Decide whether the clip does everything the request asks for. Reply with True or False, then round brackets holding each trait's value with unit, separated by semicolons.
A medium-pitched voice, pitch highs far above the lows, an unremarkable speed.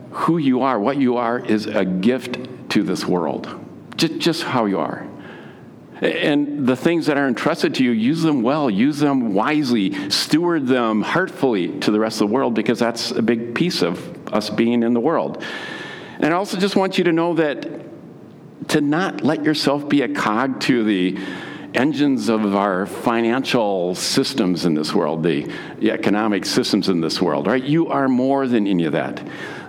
False (130 Hz; 6.0 semitones; 185 wpm)